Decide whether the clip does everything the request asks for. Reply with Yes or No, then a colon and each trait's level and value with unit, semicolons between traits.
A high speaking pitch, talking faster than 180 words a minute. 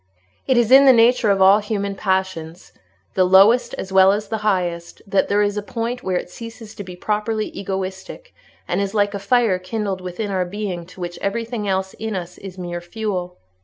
Yes: high, 200 Hz; average, 200 wpm